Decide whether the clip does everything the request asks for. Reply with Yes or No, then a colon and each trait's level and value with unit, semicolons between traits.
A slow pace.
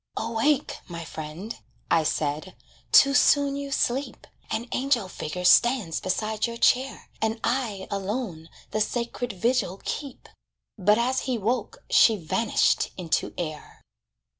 Yes: slow, 130 wpm